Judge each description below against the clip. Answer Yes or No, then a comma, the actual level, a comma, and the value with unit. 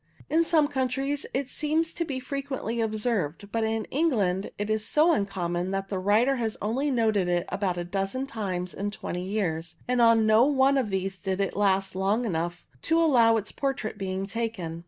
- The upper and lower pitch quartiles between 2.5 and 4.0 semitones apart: No, wide, 5.4 semitones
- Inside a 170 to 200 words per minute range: Yes, average, 195 wpm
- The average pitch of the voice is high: Yes, high, 215 Hz